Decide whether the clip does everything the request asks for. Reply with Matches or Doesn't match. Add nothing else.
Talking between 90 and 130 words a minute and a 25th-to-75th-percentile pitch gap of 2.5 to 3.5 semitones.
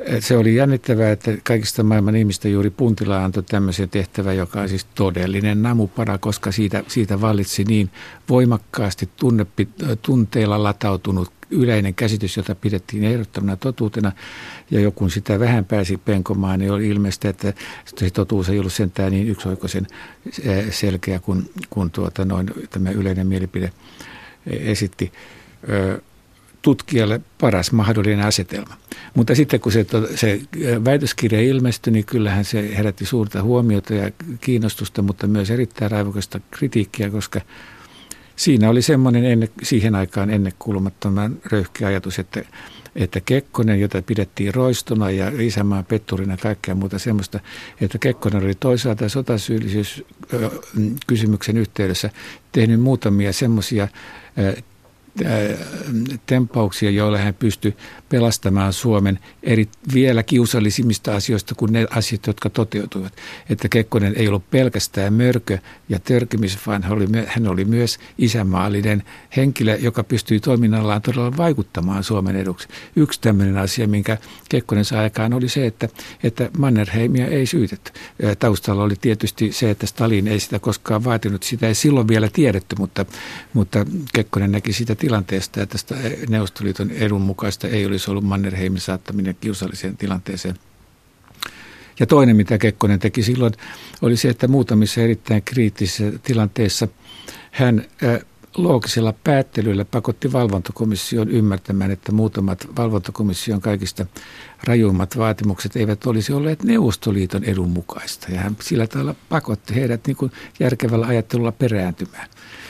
Matches